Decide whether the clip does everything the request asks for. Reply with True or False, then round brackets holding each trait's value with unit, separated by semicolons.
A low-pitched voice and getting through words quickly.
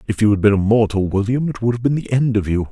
True (110 Hz; 330 wpm)